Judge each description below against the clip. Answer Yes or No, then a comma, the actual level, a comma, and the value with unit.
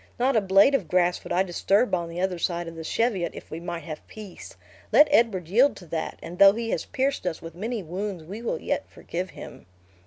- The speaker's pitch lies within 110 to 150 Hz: No, medium, 185 Hz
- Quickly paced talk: Yes, fast, 230 wpm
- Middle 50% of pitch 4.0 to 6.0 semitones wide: Yes, average, 4.5 semitones